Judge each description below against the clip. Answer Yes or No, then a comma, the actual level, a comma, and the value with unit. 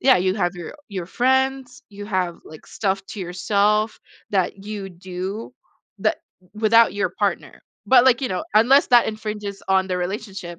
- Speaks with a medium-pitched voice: No, high, 205 Hz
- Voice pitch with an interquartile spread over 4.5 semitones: No, average, 3.4 semitones